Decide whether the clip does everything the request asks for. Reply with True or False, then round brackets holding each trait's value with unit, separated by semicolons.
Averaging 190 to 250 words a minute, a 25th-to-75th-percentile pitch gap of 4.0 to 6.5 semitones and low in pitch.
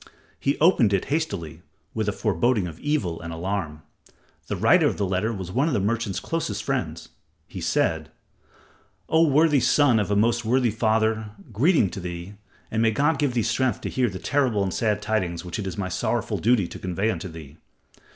True (195 wpm; 5.0 semitones; 105 Hz)